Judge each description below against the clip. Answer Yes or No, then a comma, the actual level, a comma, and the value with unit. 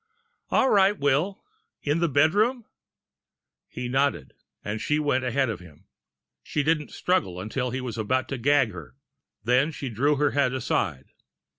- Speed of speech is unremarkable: Yes, average, 155 wpm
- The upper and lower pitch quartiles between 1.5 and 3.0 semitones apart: No, average, 4.0 semitones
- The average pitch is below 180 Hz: Yes, low, 135 Hz